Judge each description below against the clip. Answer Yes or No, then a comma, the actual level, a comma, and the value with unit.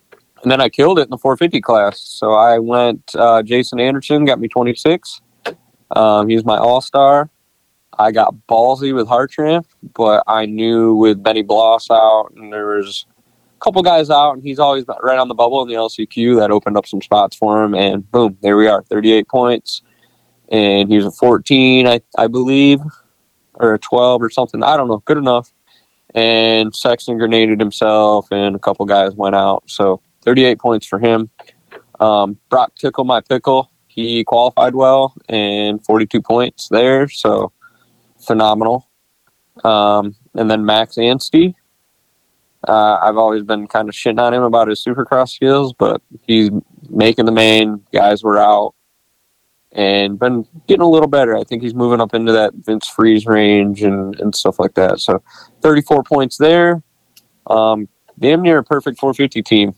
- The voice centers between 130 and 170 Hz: No, low, 115 Hz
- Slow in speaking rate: No, average, 170 wpm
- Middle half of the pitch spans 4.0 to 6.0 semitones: No, average, 3.3 semitones